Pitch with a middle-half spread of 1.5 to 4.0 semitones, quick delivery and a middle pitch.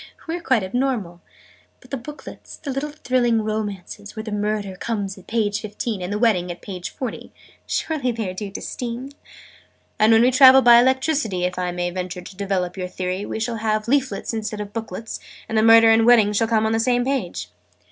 No: average, 3.7 semitones; fast, 210 wpm; high, 220 Hz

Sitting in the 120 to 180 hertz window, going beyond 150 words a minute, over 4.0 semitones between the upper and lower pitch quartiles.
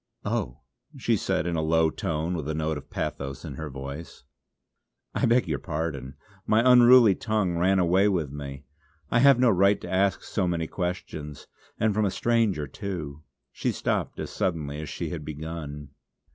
No: very low, 85 Hz; average, 175 wpm; average, 4.9 semitones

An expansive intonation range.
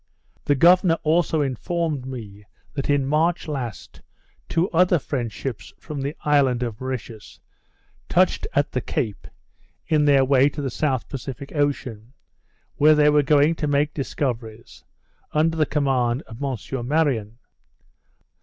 No: average, 3.4 semitones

